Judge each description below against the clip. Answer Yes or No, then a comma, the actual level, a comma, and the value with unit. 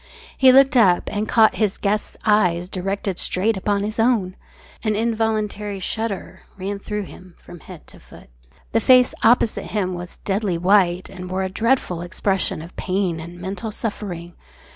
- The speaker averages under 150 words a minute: No, average, 165 wpm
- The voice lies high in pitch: Yes, high, 200 Hz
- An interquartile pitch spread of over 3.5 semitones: No, average, 3.0 semitones